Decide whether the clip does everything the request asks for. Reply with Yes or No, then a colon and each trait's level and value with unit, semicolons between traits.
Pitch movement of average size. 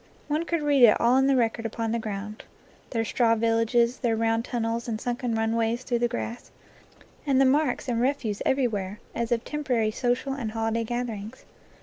No: narrow, 2.0 semitones